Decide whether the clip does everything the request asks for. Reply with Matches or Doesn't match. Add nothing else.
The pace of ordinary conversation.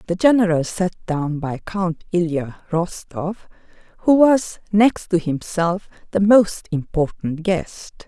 Doesn't match